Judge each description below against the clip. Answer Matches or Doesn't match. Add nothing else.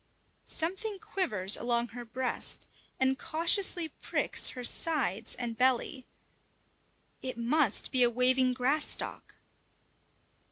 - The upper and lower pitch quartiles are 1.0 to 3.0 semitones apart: Doesn't match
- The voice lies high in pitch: Matches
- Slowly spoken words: Matches